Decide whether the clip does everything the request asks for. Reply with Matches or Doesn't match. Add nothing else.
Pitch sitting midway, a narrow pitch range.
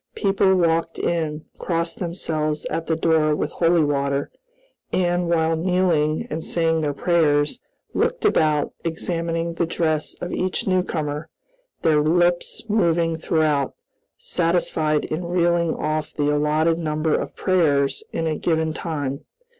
Matches